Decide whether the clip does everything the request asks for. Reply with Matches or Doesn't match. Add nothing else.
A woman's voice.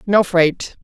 Matches